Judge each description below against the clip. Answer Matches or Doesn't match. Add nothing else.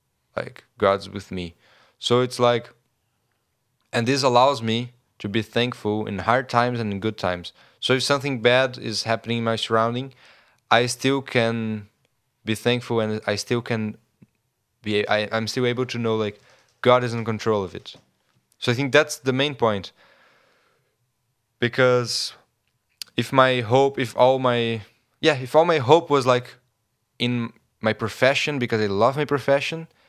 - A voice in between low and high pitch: Doesn't match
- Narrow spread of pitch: Matches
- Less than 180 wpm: Matches